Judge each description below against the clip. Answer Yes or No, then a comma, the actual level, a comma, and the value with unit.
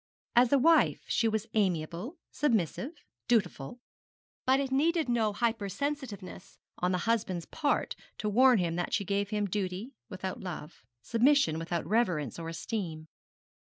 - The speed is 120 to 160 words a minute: Yes, average, 140 wpm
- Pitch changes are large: Yes, wide, 5.7 semitones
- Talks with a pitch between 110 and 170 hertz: No, high, 210 Hz